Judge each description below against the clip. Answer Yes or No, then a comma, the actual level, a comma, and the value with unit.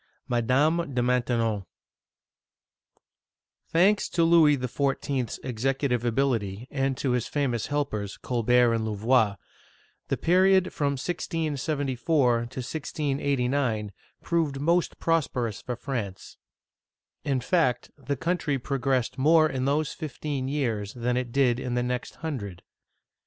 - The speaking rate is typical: No, slow, 115 wpm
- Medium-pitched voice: No, low, 130 Hz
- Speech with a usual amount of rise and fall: Yes, average, 3.5 semitones